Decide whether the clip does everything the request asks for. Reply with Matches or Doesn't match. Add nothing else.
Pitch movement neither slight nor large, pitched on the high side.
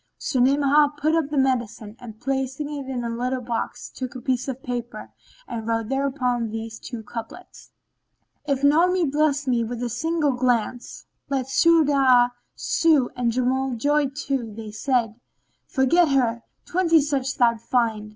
Matches